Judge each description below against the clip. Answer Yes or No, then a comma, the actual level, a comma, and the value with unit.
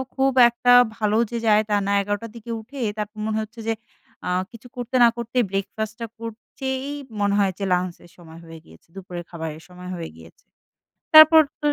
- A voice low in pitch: No, high, 215 Hz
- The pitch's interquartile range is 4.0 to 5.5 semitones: Yes, average, 4.7 semitones